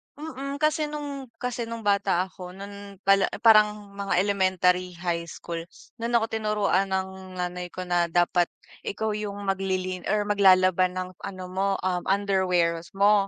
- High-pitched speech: Yes, high, 195 Hz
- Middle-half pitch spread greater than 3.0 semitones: No, narrow, 2.5 semitones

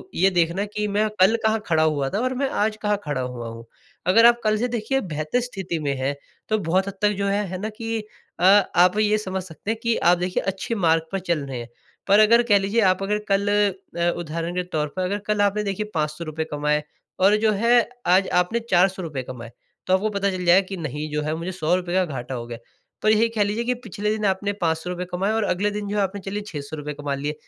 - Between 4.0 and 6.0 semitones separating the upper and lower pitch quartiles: Yes, average, 4.7 semitones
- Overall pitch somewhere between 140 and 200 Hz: Yes, high, 190 Hz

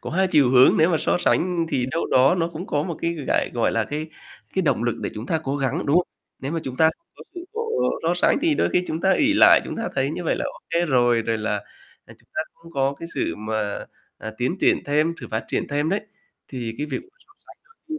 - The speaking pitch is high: No, medium, 150 Hz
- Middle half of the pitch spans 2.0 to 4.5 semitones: No, average, 5.3 semitones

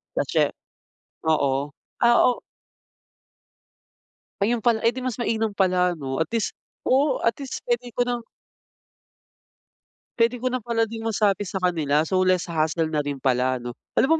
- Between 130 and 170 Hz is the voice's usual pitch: No, high, 205 Hz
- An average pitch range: No, wide, 7.1 semitones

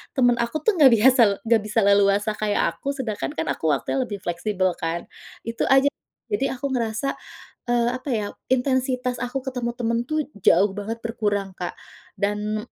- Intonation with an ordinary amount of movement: Yes, average, 3.7 semitones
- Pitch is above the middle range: Yes, high, 230 Hz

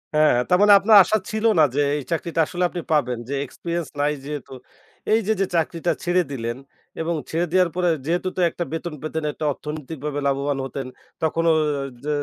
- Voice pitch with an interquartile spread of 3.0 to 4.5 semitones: Yes, average, 3.3 semitones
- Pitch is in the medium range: Yes, medium, 160 Hz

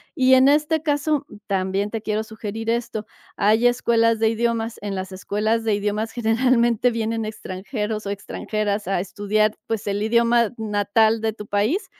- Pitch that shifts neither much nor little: No, narrow, 2.1 semitones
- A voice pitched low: No, high, 220 Hz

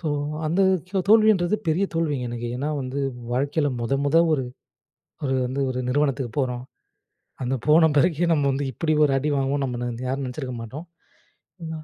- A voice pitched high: No, medium, 140 Hz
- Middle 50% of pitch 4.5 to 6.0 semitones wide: No, average, 4.0 semitones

